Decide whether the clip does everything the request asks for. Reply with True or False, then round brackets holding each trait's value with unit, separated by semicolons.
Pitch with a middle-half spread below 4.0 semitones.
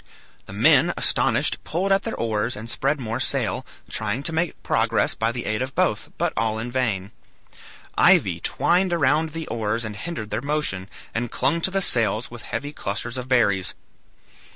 False (5.5 semitones)